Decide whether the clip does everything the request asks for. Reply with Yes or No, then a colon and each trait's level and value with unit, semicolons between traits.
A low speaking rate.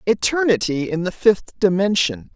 Yes: slow, 130 wpm